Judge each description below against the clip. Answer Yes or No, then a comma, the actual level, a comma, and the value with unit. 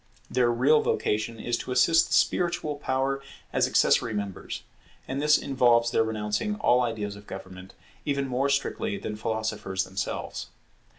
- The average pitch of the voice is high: No, low, 120 Hz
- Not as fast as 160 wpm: Yes, average, 145 wpm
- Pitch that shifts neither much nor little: Yes, average, 4.8 semitones